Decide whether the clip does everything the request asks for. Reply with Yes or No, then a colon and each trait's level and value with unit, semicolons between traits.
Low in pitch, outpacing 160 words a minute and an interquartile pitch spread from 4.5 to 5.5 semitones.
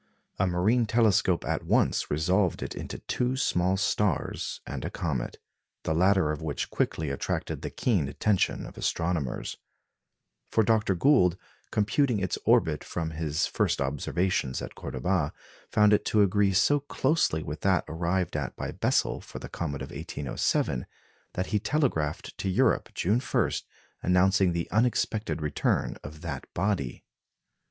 No: very low, 90 Hz; average, 145 wpm; average, 5.1 semitones